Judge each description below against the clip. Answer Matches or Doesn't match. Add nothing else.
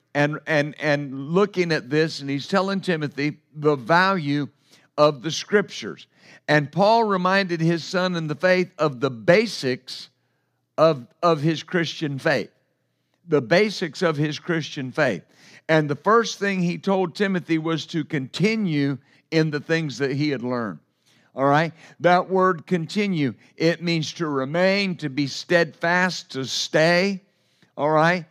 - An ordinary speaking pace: Matches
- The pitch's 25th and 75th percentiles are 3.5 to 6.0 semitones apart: Matches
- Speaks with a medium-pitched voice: Matches